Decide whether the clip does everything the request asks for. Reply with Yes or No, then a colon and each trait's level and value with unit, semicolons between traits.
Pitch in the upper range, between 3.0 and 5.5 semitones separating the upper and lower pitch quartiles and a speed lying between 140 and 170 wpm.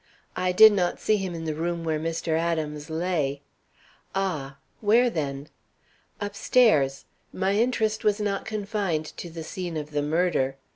No: medium, 170 Hz; average, 4.8 semitones; average, 150 wpm